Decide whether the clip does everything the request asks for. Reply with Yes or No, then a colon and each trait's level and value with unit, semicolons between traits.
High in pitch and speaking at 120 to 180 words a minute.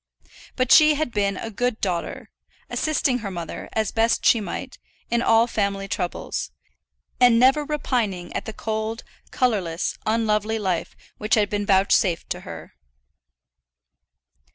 Yes: high, 220 Hz; slow, 135 wpm